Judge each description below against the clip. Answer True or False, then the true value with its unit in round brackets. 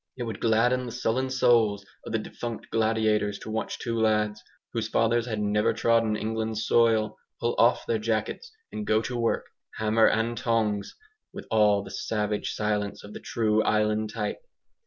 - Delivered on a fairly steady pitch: True (1.4 semitones)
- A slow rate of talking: False (170 wpm)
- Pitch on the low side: True (110 Hz)